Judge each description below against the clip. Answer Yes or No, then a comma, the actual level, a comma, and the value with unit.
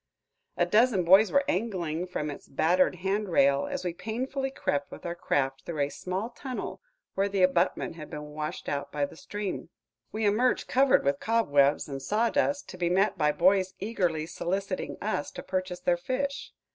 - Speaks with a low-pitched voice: No, medium, 185 Hz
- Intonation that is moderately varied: No, wide, 5.9 semitones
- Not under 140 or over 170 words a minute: No, average, 180 wpm